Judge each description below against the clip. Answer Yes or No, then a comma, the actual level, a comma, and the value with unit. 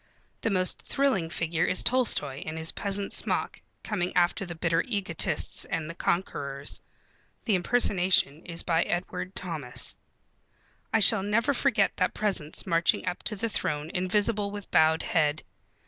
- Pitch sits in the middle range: Yes, medium, 180 Hz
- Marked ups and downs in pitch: No, average, 4.0 semitones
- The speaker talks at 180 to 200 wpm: No, average, 145 wpm